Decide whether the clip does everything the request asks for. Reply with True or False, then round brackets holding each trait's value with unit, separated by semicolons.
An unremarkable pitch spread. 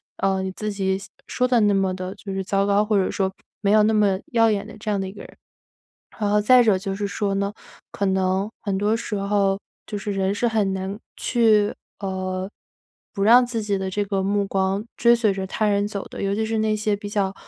False (1.7 semitones)